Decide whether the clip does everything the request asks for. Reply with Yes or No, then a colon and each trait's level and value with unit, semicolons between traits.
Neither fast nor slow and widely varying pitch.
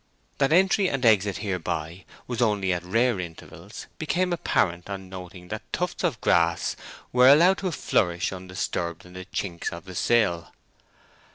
Yes: average, 155 wpm; wide, 6.0 semitones